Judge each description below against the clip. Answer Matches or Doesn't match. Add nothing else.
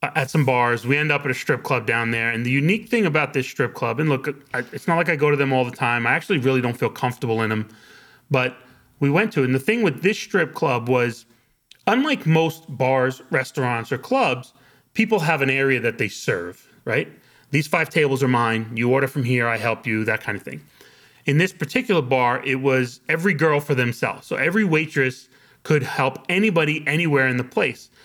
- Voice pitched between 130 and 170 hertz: Matches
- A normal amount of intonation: Matches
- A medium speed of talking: Doesn't match